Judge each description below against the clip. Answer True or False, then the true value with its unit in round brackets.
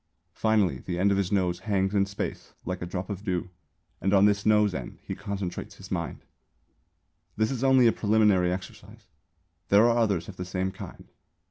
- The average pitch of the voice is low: True (100 Hz)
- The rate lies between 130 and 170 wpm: False (190 wpm)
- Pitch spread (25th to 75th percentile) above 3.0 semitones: False (2.4 semitones)